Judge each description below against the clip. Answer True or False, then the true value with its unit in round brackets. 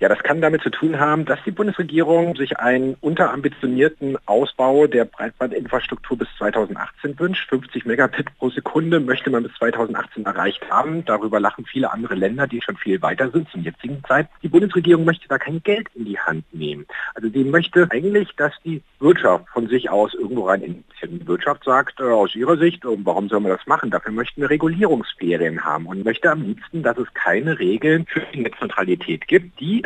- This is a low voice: False (150 Hz)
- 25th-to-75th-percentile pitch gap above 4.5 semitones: True (4.9 semitones)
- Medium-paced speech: False (195 wpm)